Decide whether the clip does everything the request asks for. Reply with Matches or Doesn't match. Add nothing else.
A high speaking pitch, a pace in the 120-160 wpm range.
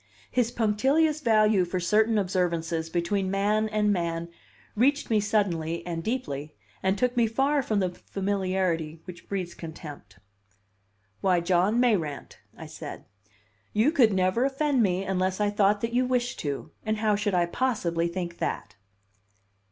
Matches